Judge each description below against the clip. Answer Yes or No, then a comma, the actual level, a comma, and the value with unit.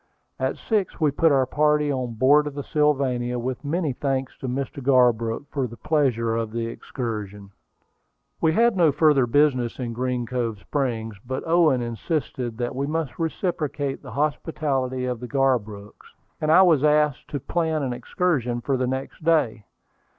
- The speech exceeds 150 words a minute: Yes, average, 165 wpm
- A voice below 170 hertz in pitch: Yes, low, 135 Hz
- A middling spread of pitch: Yes, average, 3.7 semitones